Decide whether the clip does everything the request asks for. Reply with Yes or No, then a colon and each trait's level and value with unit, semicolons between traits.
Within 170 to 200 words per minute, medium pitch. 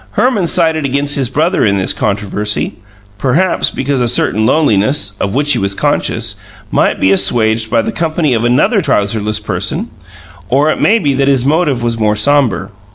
No: average, 175 wpm; low, 130 Hz